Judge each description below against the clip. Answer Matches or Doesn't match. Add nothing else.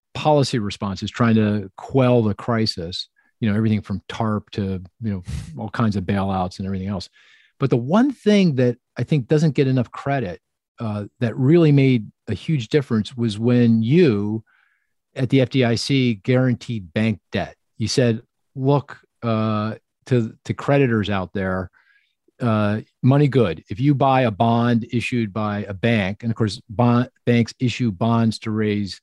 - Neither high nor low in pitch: Doesn't match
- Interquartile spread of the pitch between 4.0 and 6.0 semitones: Doesn't match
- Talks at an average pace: Matches